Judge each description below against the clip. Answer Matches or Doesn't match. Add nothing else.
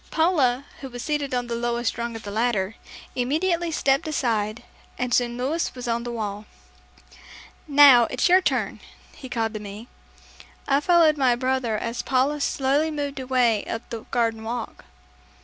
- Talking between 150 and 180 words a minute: Matches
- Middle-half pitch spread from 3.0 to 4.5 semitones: Matches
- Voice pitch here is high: Matches